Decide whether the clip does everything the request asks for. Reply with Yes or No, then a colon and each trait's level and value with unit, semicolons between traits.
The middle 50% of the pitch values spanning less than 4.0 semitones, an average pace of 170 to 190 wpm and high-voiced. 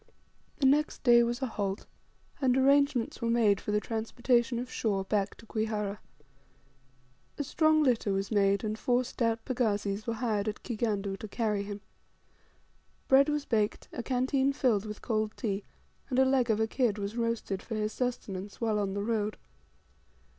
Yes: average, 3.3 semitones; average, 175 wpm; high, 225 Hz